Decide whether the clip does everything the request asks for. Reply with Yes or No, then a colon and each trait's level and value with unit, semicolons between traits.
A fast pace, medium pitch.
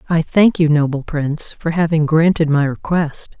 No: average, 175 wpm; medium, 155 Hz